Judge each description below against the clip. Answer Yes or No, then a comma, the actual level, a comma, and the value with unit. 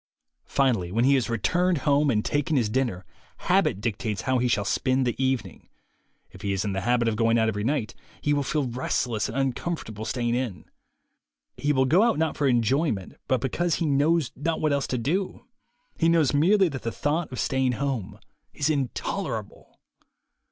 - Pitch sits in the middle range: No, low, 130 Hz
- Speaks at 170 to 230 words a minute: Yes, average, 185 wpm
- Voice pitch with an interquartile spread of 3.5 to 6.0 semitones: Yes, average, 4.3 semitones